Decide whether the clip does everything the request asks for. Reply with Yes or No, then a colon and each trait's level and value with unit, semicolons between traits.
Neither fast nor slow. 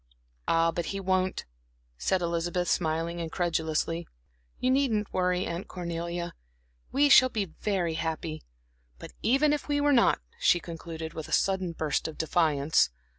Yes: average, 145 wpm